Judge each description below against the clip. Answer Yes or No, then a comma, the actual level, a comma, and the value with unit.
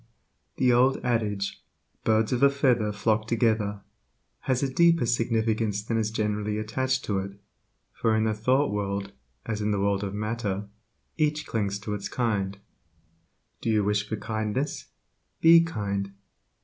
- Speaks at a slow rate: No, average, 150 wpm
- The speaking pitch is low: Yes, low, 110 Hz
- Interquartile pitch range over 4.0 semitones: No, average, 2.8 semitones